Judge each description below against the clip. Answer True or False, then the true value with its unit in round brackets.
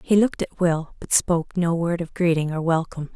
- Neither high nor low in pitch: True (170 Hz)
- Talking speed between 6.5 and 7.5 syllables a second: False (5.8 syllables/s)